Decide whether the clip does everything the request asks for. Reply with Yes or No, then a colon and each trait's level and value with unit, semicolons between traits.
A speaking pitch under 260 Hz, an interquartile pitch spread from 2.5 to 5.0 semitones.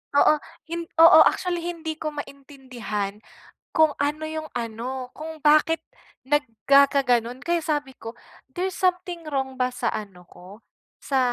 No: very high, 285 Hz; average, 4.3 semitones